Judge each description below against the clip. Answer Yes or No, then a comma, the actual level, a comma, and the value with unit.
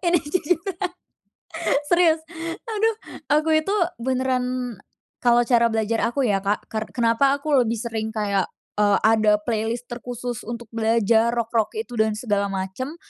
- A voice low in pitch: No, high, 235 Hz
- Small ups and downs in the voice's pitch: No, average, 3.3 semitones